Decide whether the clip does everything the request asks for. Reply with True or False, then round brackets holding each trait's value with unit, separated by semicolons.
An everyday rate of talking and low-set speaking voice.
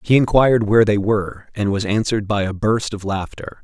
False (215 wpm; 105 Hz)